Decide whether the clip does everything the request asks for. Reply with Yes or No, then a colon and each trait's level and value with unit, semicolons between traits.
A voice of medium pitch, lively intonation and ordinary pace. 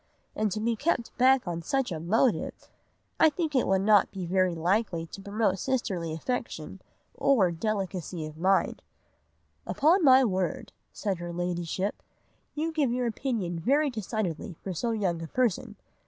No: high, 205 Hz; wide, 6.1 semitones; average, 155 wpm